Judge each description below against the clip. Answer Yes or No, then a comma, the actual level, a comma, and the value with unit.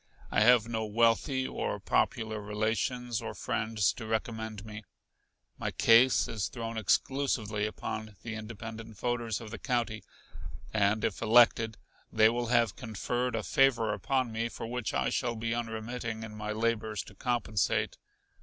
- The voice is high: No, low, 115 Hz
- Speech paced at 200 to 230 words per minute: No, average, 150 wpm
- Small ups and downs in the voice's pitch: Yes, narrow, 1.6 semitones